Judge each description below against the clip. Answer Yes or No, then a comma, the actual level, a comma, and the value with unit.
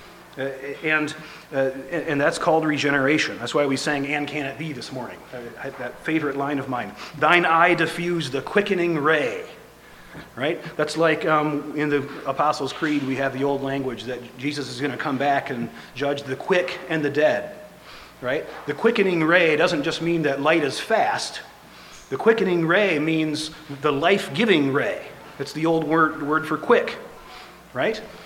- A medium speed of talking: Yes, average, 170 wpm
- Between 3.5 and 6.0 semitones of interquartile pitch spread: No, narrow, 2.5 semitones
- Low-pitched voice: No, medium, 150 Hz